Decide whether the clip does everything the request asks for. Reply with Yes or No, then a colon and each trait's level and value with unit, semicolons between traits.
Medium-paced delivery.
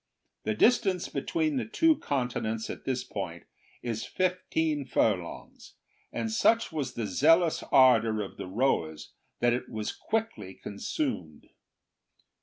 No: slow, 125 wpm